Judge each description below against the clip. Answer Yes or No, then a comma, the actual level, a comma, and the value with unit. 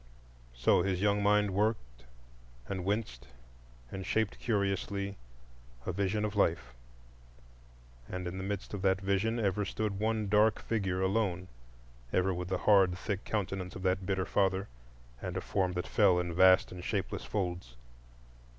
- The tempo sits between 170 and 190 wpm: No, average, 150 wpm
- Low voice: Yes, very low, 95 Hz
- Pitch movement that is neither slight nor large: No, narrow, 2.2 semitones